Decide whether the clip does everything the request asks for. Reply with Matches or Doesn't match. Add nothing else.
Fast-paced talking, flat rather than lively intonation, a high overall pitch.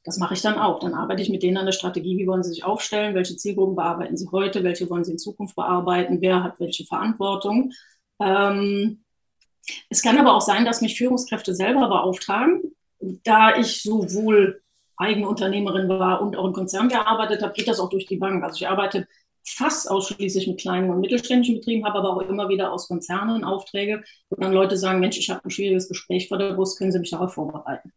Matches